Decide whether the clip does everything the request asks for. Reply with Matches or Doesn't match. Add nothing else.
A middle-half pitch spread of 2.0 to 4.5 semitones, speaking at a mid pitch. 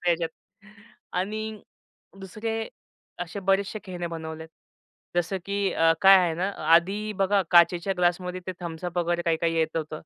Matches